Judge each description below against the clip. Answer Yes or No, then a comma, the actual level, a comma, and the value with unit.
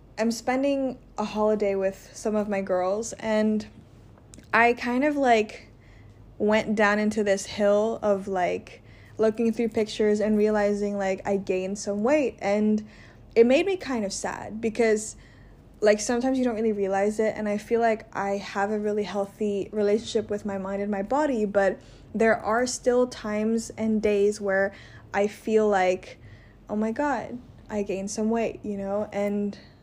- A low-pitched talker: No, high, 210 Hz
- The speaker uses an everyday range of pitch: No, narrow, 2.0 semitones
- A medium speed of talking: Yes, average, 165 wpm